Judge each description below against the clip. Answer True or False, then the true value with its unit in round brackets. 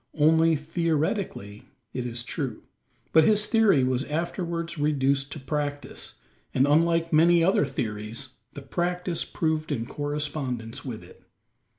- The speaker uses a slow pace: True (125 wpm)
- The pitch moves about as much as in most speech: True (4.0 semitones)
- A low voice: False (150 Hz)